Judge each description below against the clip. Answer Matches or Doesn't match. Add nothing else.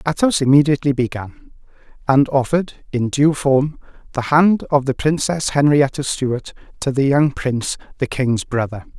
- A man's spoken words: Matches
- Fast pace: Doesn't match